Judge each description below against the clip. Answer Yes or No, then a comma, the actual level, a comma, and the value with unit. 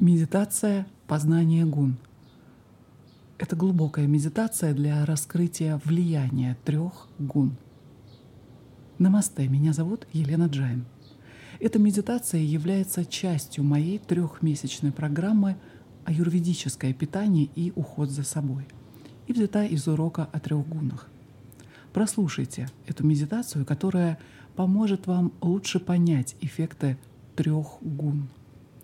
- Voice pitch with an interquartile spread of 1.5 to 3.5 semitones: No, average, 4.6 semitones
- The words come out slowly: Yes, slow, 100 wpm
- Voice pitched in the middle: Yes, medium, 155 Hz